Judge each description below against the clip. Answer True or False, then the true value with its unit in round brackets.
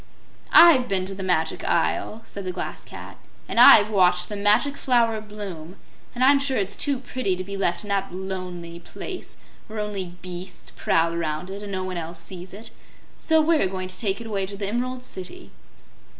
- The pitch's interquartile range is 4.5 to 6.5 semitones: False (3.6 semitones)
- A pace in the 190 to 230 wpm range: True (195 wpm)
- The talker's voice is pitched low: False (195 Hz)